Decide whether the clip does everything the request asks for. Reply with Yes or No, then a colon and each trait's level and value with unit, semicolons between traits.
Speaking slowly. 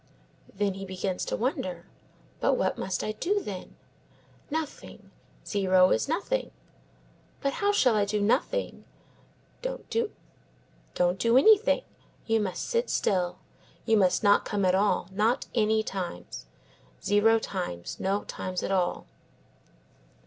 Yes: slow, 125 wpm